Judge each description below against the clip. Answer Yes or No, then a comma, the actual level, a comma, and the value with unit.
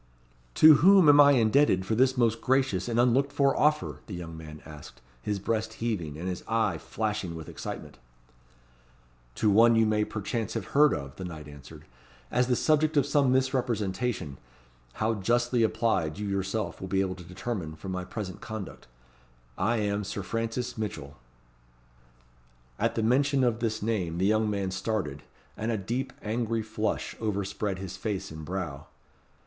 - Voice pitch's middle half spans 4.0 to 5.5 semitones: Yes, average, 4.4 semitones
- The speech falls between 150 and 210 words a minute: Yes, average, 165 wpm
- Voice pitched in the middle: No, low, 110 Hz